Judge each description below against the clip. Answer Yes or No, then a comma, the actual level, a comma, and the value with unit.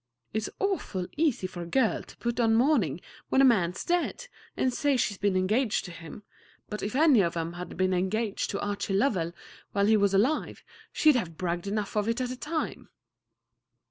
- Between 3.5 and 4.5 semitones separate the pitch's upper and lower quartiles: No, wide, 5.4 semitones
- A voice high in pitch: Yes, high, 210 Hz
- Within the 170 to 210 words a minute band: Yes, average, 200 wpm